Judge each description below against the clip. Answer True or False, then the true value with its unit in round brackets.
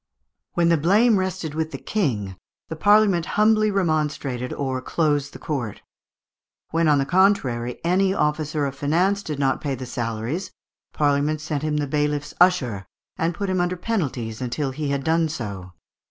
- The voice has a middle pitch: True (150 Hz)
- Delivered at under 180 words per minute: True (170 wpm)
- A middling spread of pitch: True (4.7 semitones)